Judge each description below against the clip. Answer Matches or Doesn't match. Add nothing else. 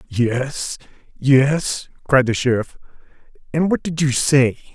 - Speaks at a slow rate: Matches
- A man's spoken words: Matches